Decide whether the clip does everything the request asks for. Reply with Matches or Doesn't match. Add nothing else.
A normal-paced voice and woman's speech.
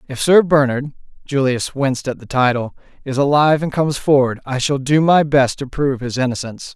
Doesn't match